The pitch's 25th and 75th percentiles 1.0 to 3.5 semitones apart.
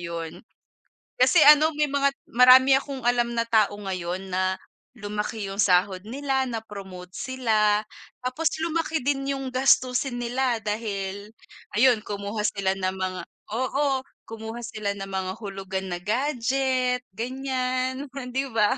No: average, 4.9 semitones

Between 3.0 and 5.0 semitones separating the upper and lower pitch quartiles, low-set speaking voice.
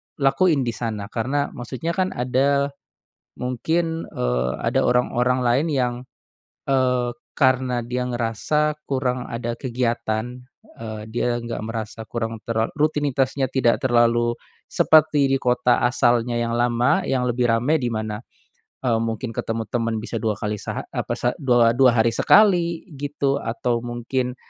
No: narrow, 2.5 semitones; low, 125 Hz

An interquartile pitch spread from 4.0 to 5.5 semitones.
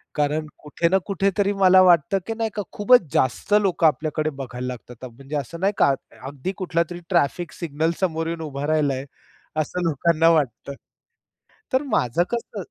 Yes: average, 4.7 semitones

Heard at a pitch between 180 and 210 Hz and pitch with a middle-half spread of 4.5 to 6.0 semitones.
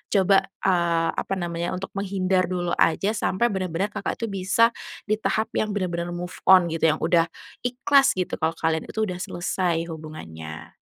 No: medium, 185 Hz; average, 2.8 semitones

